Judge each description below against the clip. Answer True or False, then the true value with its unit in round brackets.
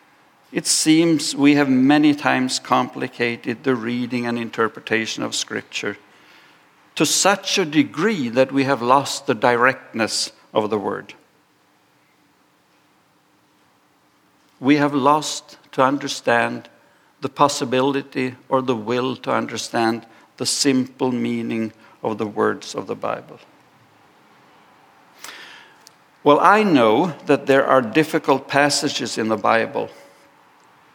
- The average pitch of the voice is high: False (135 Hz)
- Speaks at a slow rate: True (110 wpm)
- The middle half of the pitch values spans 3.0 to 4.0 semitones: True (3.5 semitones)